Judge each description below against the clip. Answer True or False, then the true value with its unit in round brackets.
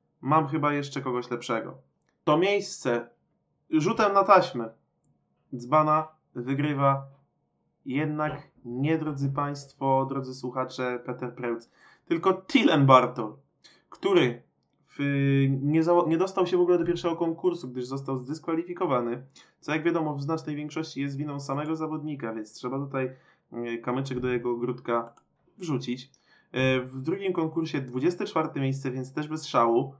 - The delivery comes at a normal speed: True (130 wpm)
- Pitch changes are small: False (4.0 semitones)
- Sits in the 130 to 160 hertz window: True (140 Hz)